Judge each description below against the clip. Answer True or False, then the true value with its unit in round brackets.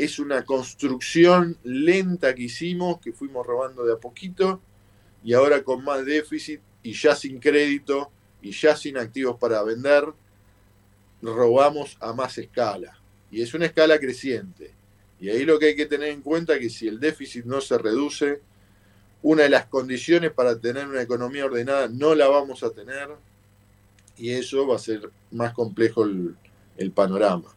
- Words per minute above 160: True (170 wpm)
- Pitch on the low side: True (125 Hz)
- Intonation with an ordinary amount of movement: False (6.3 semitones)